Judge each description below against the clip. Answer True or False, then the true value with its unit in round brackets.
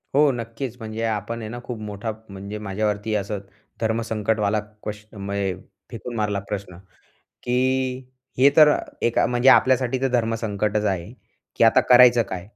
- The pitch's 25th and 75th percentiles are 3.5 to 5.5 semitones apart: False (2.9 semitones)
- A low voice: True (110 Hz)